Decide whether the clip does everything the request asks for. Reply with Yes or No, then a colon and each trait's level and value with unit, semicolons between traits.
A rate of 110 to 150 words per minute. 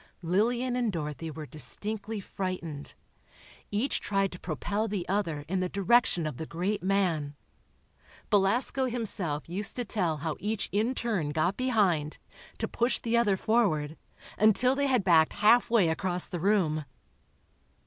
Yes: average, 145 wpm